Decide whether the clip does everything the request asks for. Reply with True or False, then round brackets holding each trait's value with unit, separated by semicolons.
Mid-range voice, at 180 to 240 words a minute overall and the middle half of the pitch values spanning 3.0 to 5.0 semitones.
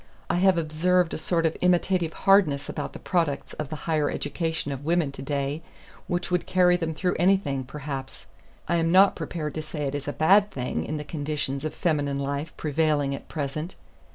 True (155 Hz; 195 wpm; 3.5 semitones)